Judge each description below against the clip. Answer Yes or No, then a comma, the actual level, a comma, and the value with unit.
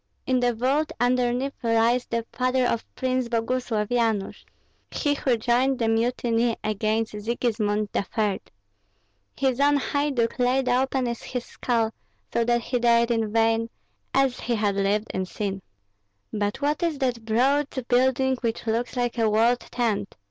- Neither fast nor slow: Yes, average, 150 wpm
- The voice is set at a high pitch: Yes, high, 240 Hz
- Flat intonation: Yes, narrow, 2.2 semitones